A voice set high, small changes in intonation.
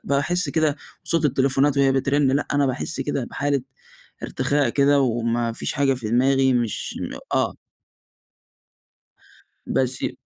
No: low, 135 Hz; narrow, 2.0 semitones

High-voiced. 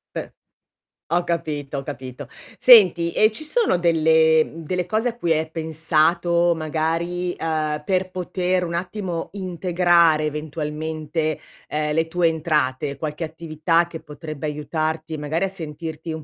No: medium, 160 Hz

